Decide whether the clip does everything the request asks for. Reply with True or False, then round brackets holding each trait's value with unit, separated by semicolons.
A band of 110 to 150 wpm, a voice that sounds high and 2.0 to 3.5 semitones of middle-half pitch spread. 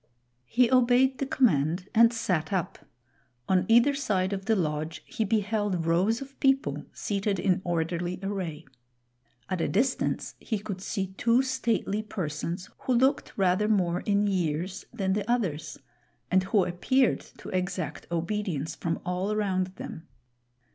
False (145 wpm; 195 Hz; 4.4 semitones)